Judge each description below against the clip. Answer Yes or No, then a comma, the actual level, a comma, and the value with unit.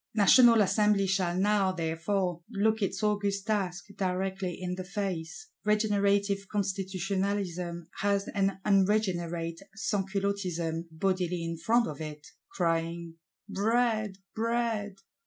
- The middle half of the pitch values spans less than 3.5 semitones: Yes, average, 2.8 semitones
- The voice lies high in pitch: Yes, high, 195 Hz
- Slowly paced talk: Yes, slow, 105 wpm